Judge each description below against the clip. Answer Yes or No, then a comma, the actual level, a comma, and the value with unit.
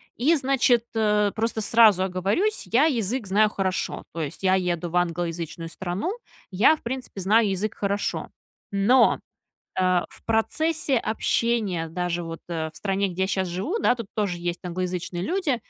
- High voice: Yes, high, 195 Hz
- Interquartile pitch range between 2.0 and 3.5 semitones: No, average, 4.6 semitones